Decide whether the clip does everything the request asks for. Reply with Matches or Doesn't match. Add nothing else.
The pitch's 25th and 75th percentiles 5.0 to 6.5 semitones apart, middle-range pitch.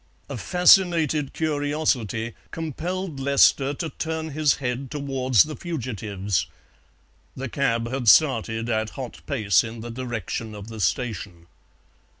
Doesn't match